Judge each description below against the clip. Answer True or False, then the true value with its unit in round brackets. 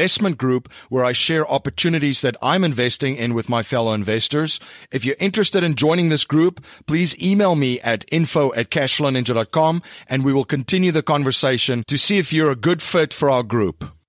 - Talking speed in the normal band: True (185 wpm)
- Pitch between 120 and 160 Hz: True (140 Hz)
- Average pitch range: True (4.5 semitones)